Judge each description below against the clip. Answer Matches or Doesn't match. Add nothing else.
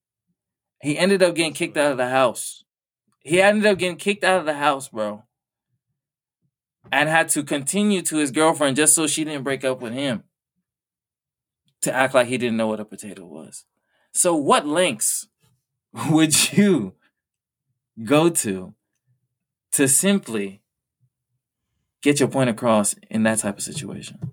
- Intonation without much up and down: Doesn't match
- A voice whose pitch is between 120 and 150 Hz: Matches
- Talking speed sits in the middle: Matches